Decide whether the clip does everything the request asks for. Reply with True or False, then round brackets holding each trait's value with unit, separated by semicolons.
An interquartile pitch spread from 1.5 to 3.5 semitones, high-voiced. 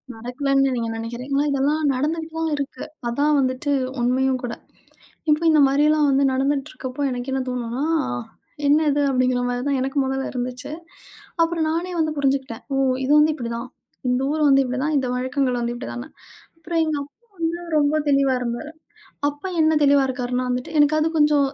True (3.0 semitones; 275 Hz)